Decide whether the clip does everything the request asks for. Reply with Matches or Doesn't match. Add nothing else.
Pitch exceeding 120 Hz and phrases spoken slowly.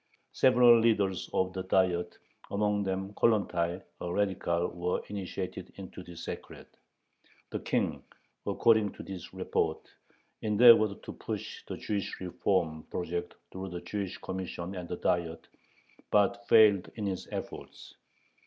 Doesn't match